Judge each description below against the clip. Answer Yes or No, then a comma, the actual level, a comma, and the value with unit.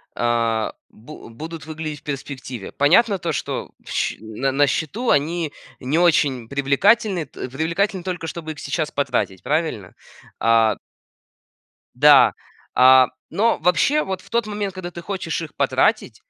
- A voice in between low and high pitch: Yes, medium, 155 Hz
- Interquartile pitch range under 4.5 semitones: No, average, 5.2 semitones